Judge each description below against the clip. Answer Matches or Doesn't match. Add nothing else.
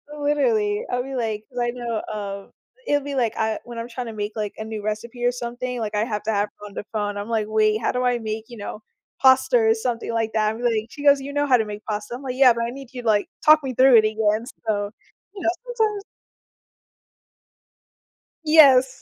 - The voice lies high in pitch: Matches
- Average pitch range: Matches